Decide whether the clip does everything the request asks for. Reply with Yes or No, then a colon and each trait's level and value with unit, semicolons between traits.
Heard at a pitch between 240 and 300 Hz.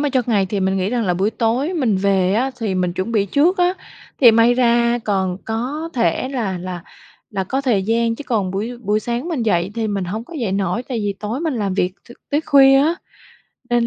No: high, 225 Hz